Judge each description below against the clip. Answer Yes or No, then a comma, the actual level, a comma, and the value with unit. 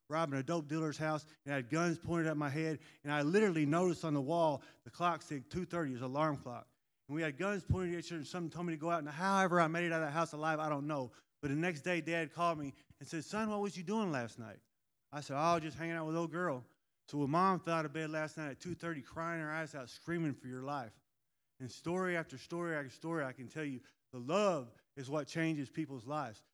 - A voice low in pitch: No, medium, 155 Hz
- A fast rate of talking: Yes, fast, 265 wpm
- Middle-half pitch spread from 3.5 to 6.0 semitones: No, average, 3.0 semitones